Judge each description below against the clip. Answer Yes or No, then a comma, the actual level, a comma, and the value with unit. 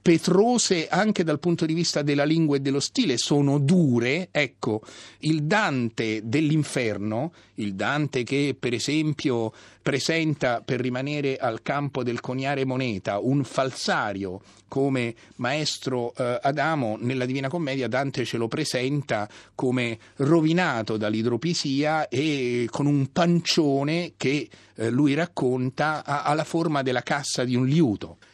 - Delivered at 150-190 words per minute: No, average, 125 wpm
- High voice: No, medium, 140 Hz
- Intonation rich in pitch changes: No, average, 4.1 semitones